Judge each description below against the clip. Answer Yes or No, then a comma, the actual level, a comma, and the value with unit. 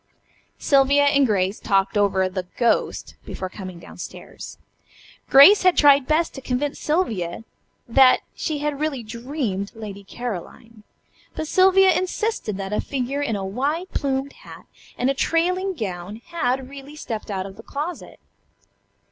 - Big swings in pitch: Yes, wide, 6.5 semitones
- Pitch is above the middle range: Yes, very high, 260 Hz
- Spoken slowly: No, average, 150 wpm